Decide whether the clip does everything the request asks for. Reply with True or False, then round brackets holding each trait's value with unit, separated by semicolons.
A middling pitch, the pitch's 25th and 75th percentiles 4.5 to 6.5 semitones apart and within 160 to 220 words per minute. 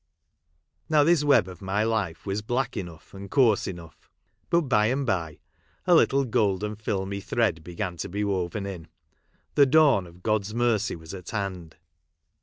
False (100 Hz; 4.8 semitones; 165 wpm)